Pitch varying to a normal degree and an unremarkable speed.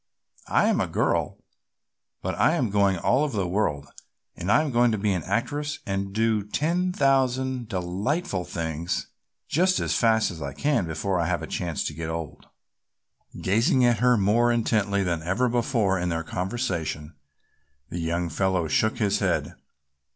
No: wide, 5.8 semitones; average, 170 wpm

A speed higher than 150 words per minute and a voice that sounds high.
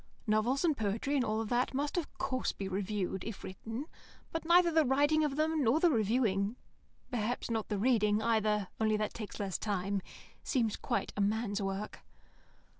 Yes: average, 175 wpm; high, 220 Hz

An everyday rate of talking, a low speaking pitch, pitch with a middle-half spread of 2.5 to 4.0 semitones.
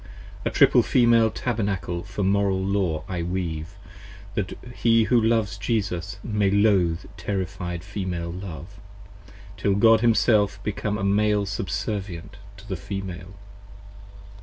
No: slow, 125 wpm; low, 100 Hz; average, 2.8 semitones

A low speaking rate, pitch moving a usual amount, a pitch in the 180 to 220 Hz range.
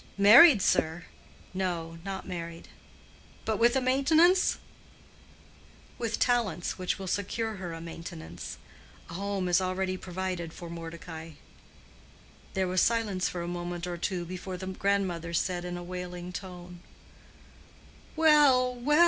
Yes: slow, 130 wpm; average, 3.1 semitones; medium, 185 Hz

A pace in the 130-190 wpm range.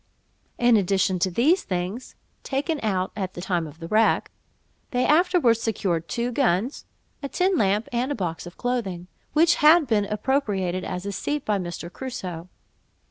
Yes: average, 165 wpm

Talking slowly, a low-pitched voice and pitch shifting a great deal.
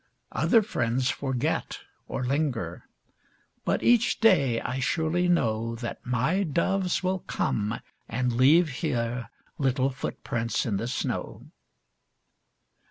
Yes: slow, 110 wpm; low, 130 Hz; wide, 6.1 semitones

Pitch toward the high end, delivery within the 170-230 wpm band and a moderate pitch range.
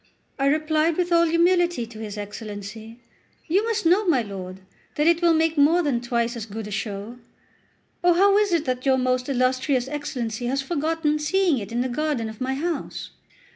No: very high, 275 Hz; average, 190 wpm; wide, 6.0 semitones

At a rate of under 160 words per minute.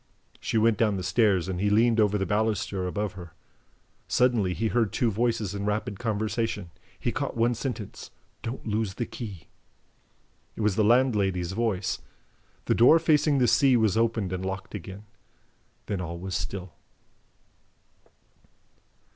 Yes: average, 150 wpm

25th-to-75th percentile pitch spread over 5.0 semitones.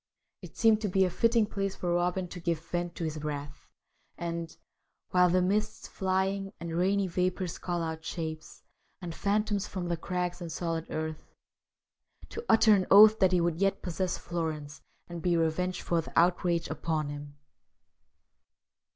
No: narrow, 2.6 semitones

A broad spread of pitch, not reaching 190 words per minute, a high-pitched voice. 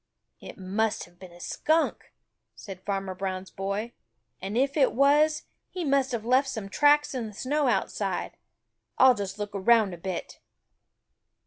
Yes: wide, 6.0 semitones; average, 155 wpm; high, 220 Hz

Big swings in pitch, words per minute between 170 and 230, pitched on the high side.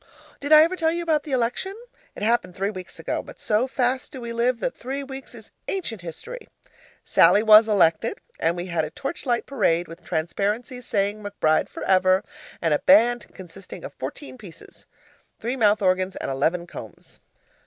Yes: wide, 6.2 semitones; average, 180 wpm; high, 215 Hz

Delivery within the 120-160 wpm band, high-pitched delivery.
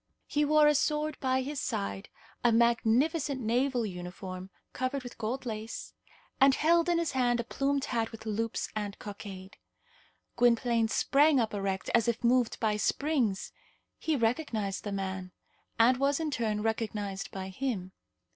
Yes: average, 155 wpm; high, 235 Hz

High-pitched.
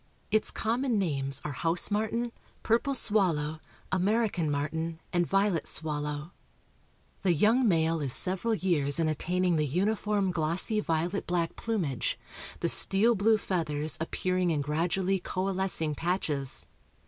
No: medium, 180 Hz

